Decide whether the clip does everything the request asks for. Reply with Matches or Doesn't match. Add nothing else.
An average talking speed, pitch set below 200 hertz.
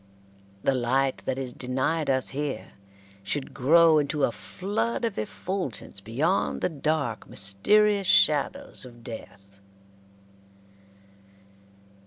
Doesn't match